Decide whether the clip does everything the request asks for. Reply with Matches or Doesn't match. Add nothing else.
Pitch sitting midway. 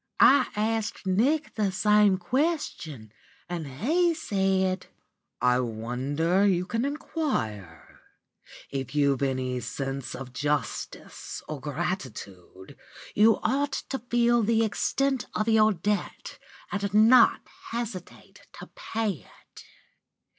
Doesn't match